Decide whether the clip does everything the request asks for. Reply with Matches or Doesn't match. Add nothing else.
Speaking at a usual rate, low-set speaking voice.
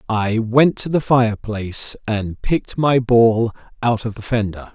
Matches